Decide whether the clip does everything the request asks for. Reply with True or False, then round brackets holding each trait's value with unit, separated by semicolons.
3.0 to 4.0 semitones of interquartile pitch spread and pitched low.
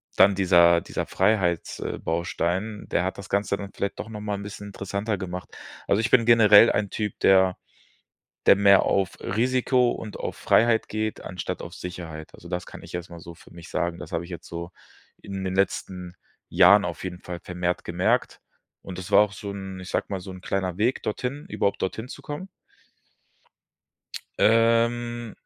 True (3.3 semitones; 100 Hz)